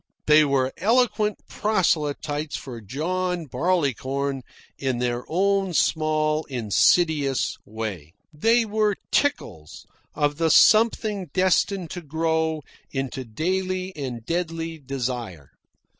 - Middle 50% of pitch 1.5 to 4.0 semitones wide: No, wide, 5.6 semitones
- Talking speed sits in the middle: No, slow, 100 wpm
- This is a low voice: No, medium, 155 Hz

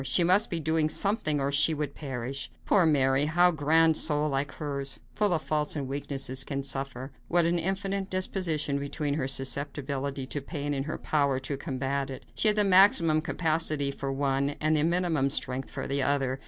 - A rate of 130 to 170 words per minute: No, average, 195 wpm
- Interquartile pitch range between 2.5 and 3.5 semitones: Yes, average, 3.0 semitones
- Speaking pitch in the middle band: Yes, medium, 145 Hz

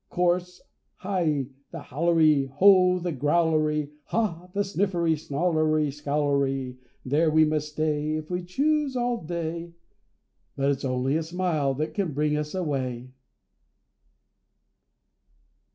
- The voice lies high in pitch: No, medium, 155 Hz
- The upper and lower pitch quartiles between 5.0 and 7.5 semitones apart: No, average, 3.3 semitones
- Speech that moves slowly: Yes, slow, 115 wpm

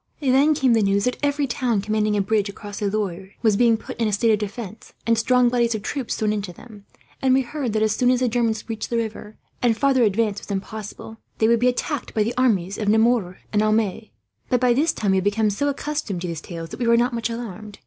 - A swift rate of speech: Yes, fast, 250 wpm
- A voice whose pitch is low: No, high, 220 Hz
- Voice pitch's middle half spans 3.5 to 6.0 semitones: No, average, 3.0 semitones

